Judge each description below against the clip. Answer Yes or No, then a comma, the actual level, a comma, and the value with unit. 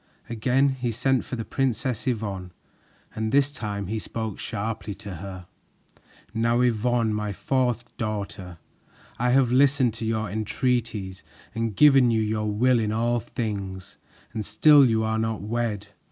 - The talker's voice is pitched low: Yes, low, 110 Hz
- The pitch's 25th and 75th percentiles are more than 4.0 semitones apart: No, average, 2.8 semitones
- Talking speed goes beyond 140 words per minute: Yes, average, 150 wpm